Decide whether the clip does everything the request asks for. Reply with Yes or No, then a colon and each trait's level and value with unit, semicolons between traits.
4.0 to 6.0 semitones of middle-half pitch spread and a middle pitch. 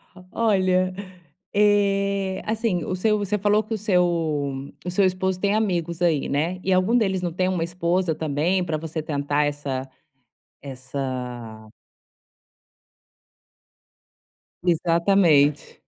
Yes: average, 4.7 semitones; medium, 180 Hz